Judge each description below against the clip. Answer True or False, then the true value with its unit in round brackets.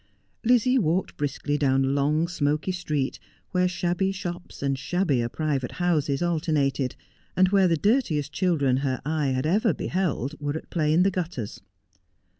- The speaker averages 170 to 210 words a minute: False (155 wpm)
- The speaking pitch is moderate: True (155 Hz)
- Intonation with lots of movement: False (4.4 semitones)